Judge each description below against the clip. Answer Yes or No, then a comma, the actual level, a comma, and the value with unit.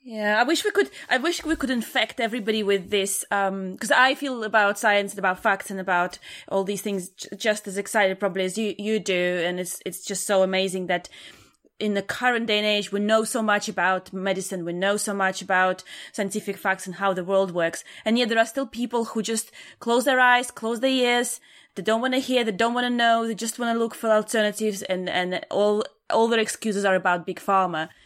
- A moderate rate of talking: No, fast, 230 wpm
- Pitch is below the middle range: No, high, 210 Hz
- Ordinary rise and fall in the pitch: Yes, average, 3.3 semitones